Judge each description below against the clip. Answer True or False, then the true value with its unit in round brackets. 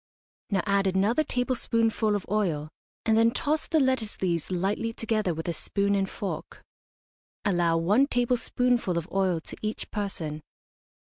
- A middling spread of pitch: True (4.1 semitones)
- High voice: True (205 Hz)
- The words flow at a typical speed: True (145 wpm)